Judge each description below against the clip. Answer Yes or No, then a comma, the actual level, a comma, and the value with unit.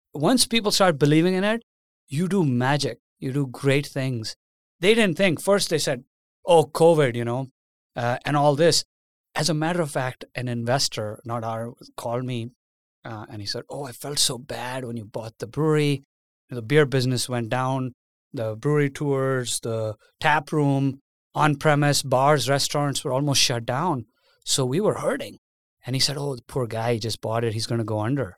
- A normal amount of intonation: Yes, average, 4.1 semitones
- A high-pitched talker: No, low, 135 Hz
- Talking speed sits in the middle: Yes, average, 195 wpm